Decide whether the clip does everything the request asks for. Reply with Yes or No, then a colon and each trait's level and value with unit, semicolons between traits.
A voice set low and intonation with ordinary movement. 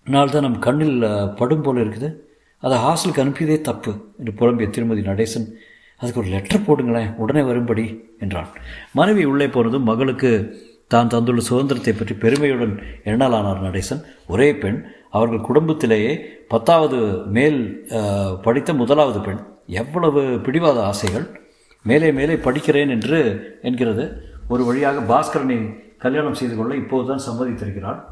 Yes: low, 120 Hz; average, 4.1 semitones